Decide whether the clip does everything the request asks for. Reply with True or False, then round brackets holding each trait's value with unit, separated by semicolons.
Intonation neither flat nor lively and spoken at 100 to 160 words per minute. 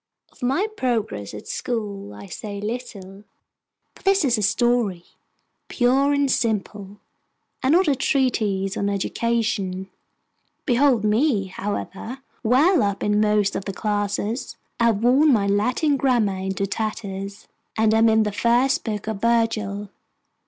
True (3.6 semitones; 140 wpm)